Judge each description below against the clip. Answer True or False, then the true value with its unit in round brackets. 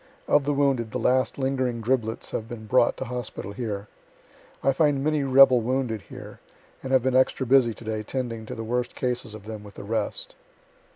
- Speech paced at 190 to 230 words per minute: True (195 wpm)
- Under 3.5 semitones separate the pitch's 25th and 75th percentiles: True (3.1 semitones)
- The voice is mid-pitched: False (125 Hz)